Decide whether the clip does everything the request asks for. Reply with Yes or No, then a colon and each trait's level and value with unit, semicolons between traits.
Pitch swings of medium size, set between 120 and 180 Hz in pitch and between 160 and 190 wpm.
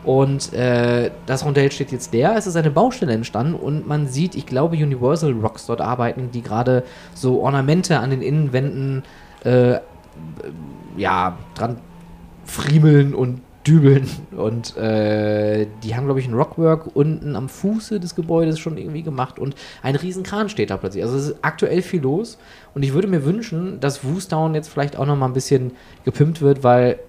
Yes: average, 4.1 semitones; medium, 140 Hz; average, 175 wpm